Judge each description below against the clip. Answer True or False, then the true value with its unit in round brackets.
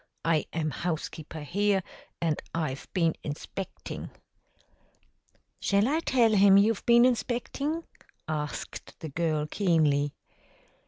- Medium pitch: True (170 Hz)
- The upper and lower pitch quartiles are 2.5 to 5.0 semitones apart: False (5.6 semitones)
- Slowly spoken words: True (105 wpm)